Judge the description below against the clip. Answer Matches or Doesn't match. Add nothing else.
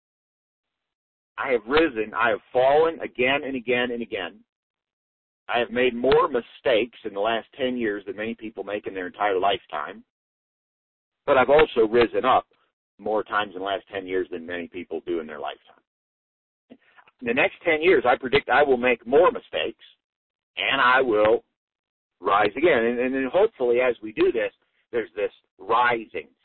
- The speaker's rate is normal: Matches